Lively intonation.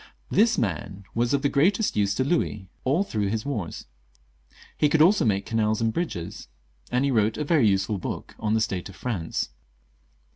Yes: wide, 6.1 semitones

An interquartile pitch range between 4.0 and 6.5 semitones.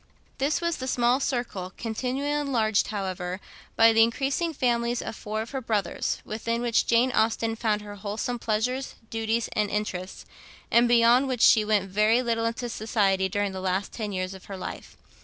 No: average, 2.9 semitones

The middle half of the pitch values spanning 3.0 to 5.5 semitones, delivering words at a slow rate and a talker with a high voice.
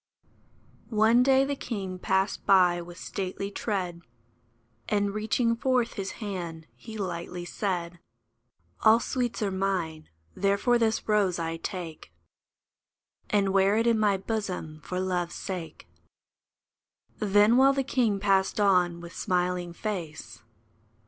Yes: average, 3.7 semitones; slow, 130 wpm; high, 195 Hz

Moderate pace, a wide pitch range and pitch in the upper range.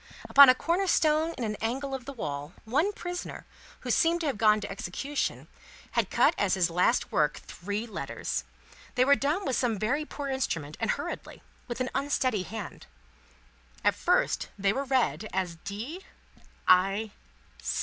Yes: average, 165 wpm; wide, 6.3 semitones; high, 235 Hz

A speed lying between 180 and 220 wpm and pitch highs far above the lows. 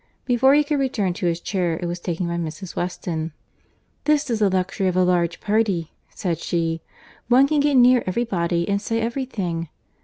Yes: average, 190 wpm; wide, 6.0 semitones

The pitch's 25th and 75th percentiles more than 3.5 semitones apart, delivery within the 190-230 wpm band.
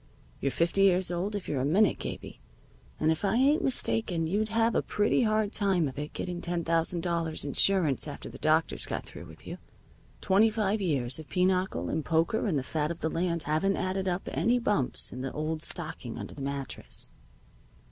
Yes: average, 4.4 semitones; average, 200 wpm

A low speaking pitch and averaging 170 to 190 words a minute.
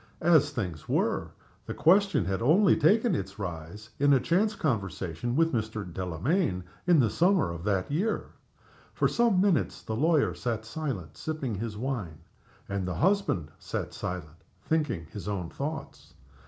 No: low, 115 Hz; average, 155 wpm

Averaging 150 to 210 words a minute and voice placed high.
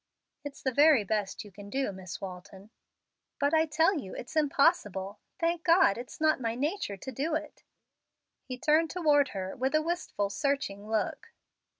Yes: average, 170 wpm; very high, 270 Hz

